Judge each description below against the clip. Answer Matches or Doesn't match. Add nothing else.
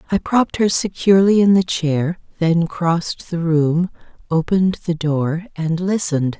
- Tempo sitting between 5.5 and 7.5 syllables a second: Doesn't match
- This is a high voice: Doesn't match